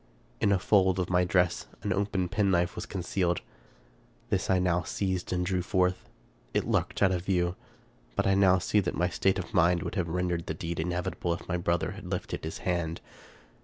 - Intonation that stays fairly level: Yes, narrow, 1.4 semitones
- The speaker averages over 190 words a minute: Yes, average, 200 wpm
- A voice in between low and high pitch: No, very low, 90 Hz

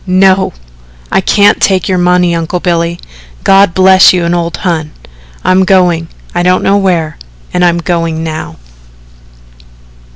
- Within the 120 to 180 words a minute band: Yes, average, 140 wpm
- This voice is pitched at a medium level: Yes, medium, 180 Hz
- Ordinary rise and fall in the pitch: No, narrow, 1.9 semitones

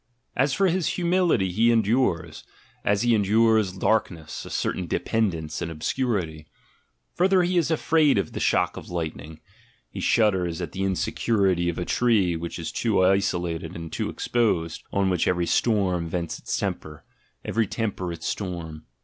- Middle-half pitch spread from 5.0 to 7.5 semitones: Yes, average, 5.3 semitones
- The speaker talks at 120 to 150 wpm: No, average, 160 wpm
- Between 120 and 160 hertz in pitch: No, very low, 95 Hz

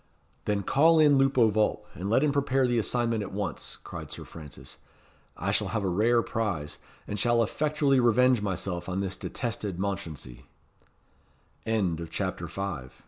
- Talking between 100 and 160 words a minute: Yes, average, 150 wpm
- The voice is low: Yes, low, 105 Hz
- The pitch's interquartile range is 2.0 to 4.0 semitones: No, average, 4.8 semitones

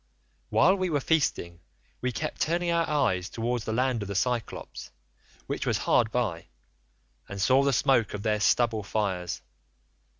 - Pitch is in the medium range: No, low, 120 Hz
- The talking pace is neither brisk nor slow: Yes, average, 160 wpm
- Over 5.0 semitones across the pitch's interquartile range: Yes, wide, 5.4 semitones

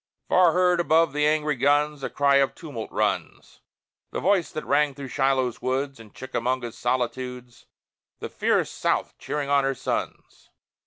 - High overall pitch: No, medium, 140 Hz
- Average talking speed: Yes, average, 155 wpm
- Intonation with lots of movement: No, average, 2.8 semitones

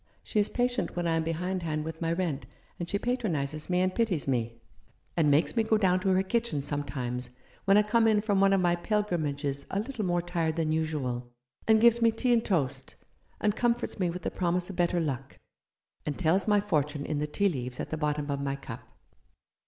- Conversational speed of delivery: No, fast, 215 wpm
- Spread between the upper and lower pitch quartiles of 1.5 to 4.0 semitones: No, wide, 5.5 semitones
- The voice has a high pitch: No, medium, 175 Hz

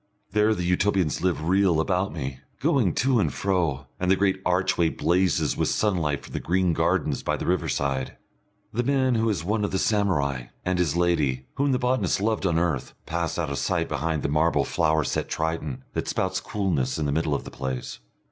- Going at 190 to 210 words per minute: Yes, average, 200 wpm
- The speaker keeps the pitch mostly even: No, average, 4.3 semitones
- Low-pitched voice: Yes, very low, 85 Hz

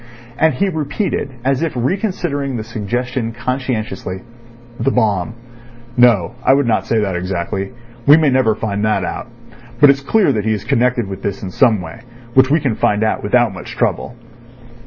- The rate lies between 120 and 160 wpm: No, average, 180 wpm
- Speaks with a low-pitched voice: Yes, low, 120 Hz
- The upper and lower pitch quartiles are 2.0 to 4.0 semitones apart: No, average, 4.7 semitones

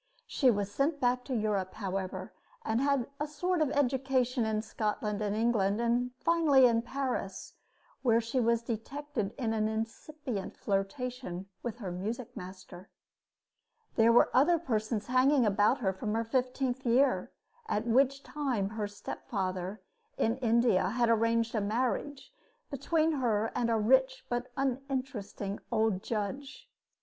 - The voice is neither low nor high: No, high, 235 Hz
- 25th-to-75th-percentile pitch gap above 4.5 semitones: No, average, 3.8 semitones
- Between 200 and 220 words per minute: No, average, 140 wpm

